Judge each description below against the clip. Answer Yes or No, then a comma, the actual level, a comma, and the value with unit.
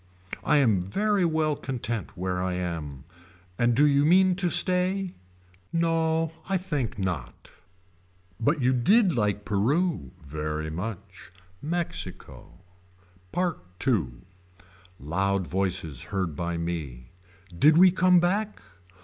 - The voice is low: Yes, low, 120 Hz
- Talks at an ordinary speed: No, slow, 115 wpm